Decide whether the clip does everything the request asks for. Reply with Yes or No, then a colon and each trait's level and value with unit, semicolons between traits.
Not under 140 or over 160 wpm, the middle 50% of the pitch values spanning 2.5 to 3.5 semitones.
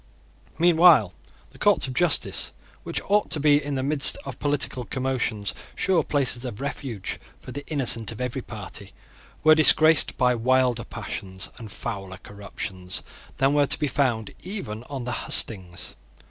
No: average, 155 wpm; average, 5.0 semitones